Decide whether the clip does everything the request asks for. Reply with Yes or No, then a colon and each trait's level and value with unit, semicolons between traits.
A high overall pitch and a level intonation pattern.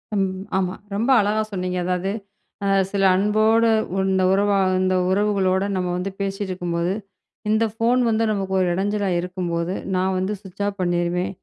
Yes: high, 195 Hz; narrow, 2.1 semitones